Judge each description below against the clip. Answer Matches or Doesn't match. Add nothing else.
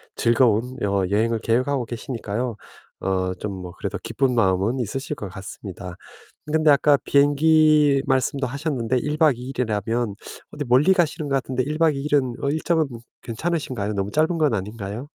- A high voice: Doesn't match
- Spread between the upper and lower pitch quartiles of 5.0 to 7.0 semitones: Matches